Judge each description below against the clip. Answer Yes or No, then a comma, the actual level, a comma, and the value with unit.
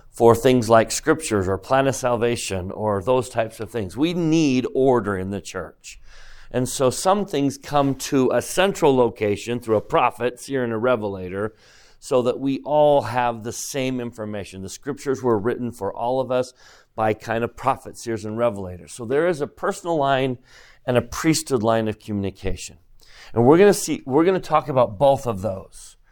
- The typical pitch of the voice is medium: No, low, 120 Hz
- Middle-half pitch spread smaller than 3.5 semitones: No, average, 3.9 semitones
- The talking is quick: No, average, 190 wpm